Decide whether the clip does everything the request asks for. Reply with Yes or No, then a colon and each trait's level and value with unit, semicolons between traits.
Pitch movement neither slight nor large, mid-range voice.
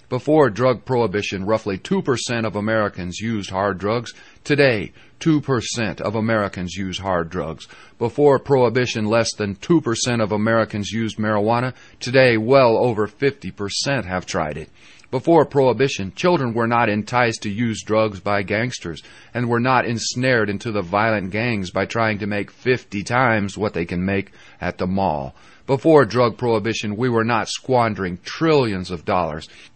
No: average, 3.7 semitones; low, 110 Hz